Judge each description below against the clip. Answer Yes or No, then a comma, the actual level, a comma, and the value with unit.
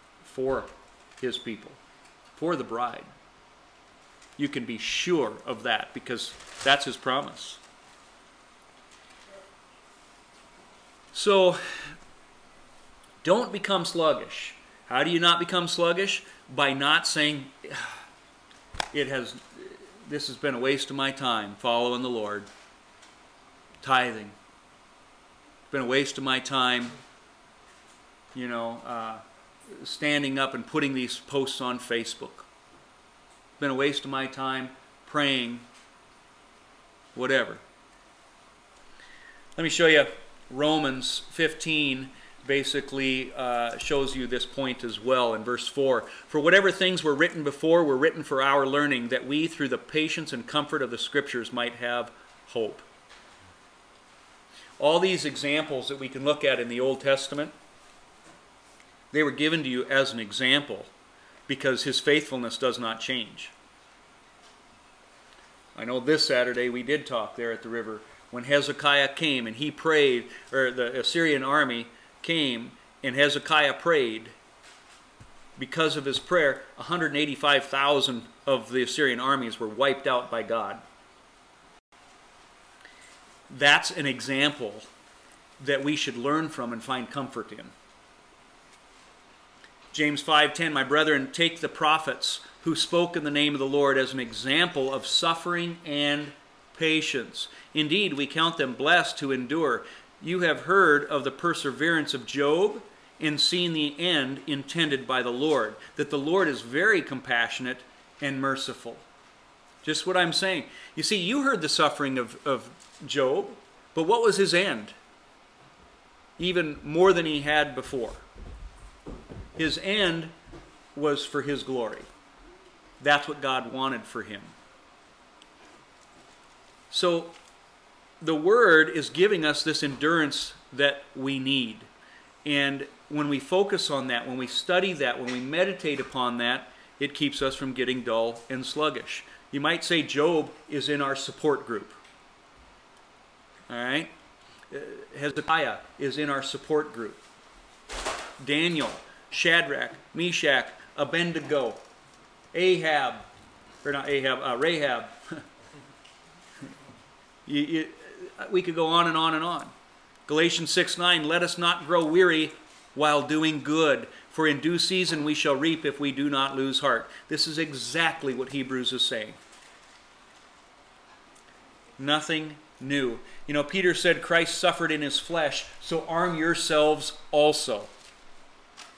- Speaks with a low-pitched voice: No, medium, 145 Hz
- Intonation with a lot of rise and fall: No, average, 3.4 semitones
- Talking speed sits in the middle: No, slow, 130 wpm